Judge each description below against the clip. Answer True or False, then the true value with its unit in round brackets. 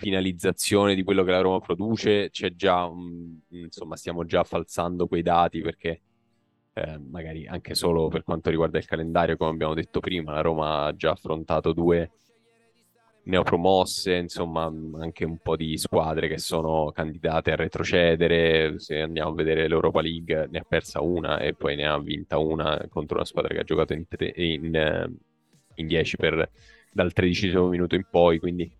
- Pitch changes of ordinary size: False (2.1 semitones)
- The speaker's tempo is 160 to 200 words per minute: True (165 wpm)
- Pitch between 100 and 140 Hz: False (85 Hz)